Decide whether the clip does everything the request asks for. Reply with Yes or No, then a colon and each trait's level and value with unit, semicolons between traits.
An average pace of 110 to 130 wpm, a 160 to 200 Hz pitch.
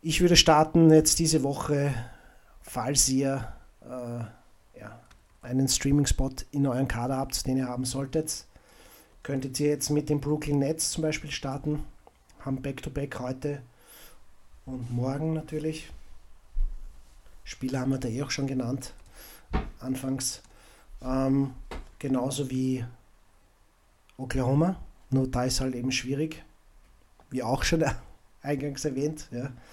No: slow, 125 wpm; low, 135 Hz